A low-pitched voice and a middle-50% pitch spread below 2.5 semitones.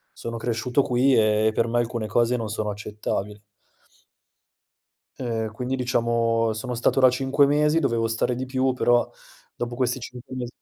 Yes: low, 120 Hz; narrow, 2.1 semitones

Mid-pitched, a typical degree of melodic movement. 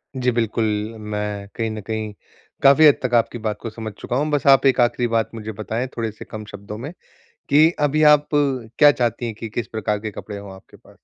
No: low, 115 Hz; average, 3.5 semitones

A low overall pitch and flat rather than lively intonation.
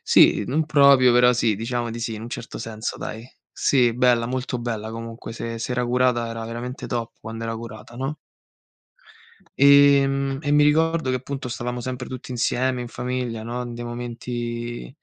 Yes: low, 120 Hz; narrow, 1.8 semitones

